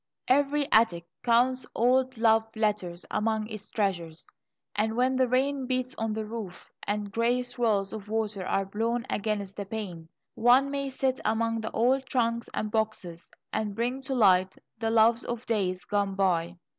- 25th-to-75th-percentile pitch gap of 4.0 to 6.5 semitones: No, average, 3.5 semitones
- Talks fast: No, average, 165 wpm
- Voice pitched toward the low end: No, high, 220 Hz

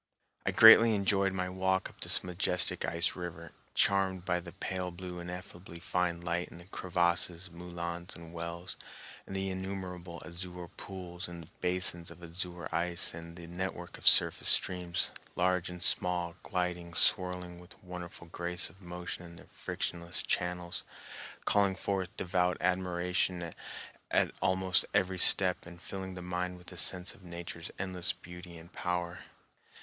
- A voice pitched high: No, very low, 90 Hz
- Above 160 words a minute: No, average, 150 wpm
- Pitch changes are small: Yes, narrow, 1.2 semitones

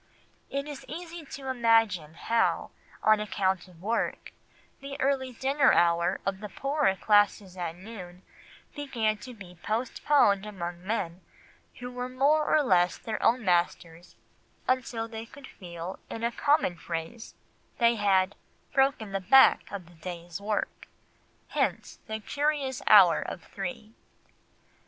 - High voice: Yes, high, 215 Hz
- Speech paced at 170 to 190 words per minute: No, average, 140 wpm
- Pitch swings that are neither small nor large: No, wide, 6.0 semitones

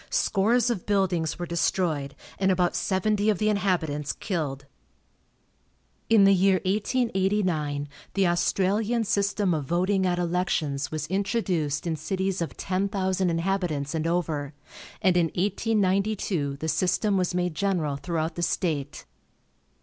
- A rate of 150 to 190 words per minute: No, slow, 135 wpm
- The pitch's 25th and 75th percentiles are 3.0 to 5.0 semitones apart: Yes, average, 3.5 semitones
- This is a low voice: No, medium, 180 Hz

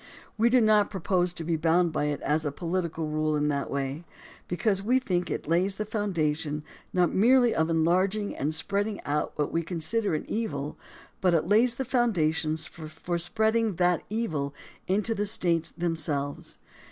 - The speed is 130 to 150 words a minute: No, average, 170 wpm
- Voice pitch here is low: No, medium, 175 Hz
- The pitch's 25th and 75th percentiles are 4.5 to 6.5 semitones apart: Yes, average, 5.1 semitones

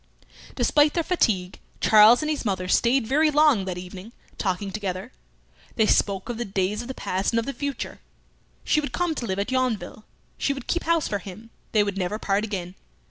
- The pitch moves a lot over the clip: Yes, wide, 5.8 semitones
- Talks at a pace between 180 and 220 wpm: Yes, average, 200 wpm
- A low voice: No, high, 220 Hz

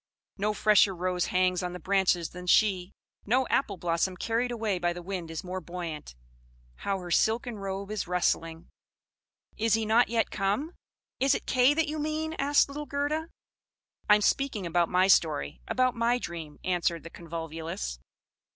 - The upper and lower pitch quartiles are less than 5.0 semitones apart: No, average, 5.3 semitones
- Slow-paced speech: No, average, 165 wpm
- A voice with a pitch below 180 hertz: No, high, 190 Hz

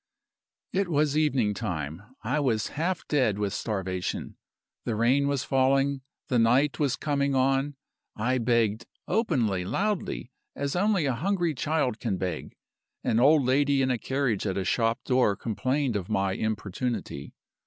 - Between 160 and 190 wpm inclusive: No, average, 150 wpm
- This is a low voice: Yes, low, 130 Hz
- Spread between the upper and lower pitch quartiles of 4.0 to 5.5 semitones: Yes, average, 4.8 semitones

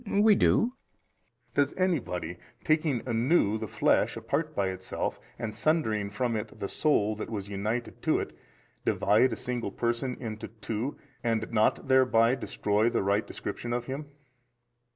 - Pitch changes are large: No, average, 3.7 semitones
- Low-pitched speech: Yes, low, 115 Hz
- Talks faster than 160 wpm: No, average, 155 wpm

